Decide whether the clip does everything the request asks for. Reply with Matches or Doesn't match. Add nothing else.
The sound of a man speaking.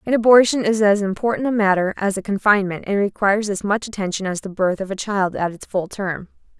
Doesn't match